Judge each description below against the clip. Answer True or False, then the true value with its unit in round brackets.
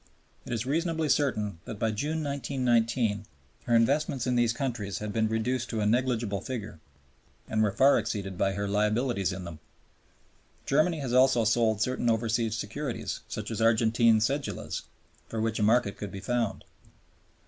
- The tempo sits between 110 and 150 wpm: False (160 wpm)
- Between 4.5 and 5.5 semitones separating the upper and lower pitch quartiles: False (3.2 semitones)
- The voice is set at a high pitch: False (115 Hz)